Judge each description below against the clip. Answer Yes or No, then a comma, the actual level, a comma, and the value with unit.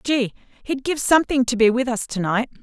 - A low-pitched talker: No, very high, 250 Hz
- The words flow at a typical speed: No, fast, 230 wpm